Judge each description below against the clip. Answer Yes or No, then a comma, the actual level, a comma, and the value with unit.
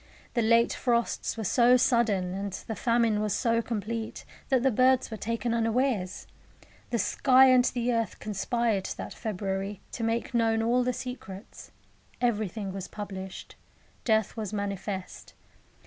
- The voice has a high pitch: Yes, high, 225 Hz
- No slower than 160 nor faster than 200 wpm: No, average, 145 wpm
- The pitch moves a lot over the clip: No, average, 2.9 semitones